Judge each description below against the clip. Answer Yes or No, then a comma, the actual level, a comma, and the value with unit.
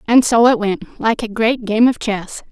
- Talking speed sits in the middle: No, fast, 240 wpm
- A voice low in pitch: No, high, 225 Hz